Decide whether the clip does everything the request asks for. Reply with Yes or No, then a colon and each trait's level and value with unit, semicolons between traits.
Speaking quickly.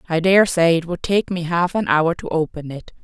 Yes: fast, 255 wpm